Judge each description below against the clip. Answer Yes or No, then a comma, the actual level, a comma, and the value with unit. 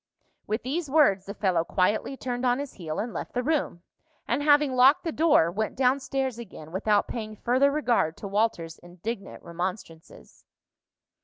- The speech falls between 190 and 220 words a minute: No, average, 165 wpm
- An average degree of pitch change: No, wide, 6.2 semitones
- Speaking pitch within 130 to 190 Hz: No, high, 230 Hz